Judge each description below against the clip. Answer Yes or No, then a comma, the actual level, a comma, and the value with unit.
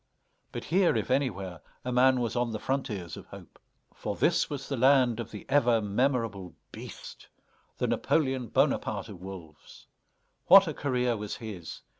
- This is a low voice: Yes, low, 120 Hz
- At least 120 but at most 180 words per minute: Yes, average, 160 wpm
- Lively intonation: No, average, 4.5 semitones